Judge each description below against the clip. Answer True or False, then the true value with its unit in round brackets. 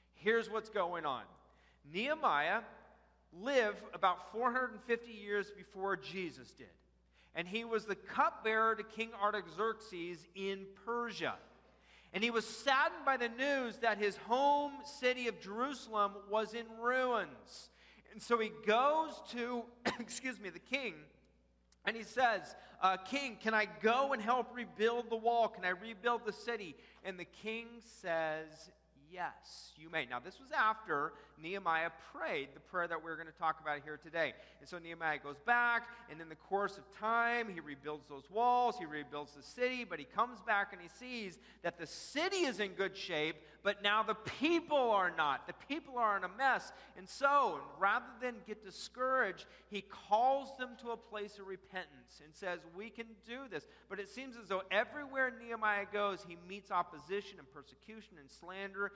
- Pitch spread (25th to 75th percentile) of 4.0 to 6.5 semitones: True (4.7 semitones)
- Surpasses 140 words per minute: True (170 wpm)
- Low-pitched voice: False (210 Hz)